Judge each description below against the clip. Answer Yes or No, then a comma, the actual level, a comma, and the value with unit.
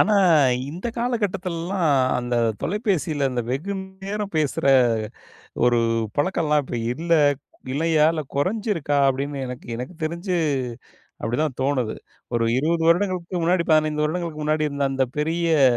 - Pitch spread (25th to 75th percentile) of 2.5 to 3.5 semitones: No, average, 4.3 semitones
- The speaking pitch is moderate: Yes, medium, 155 Hz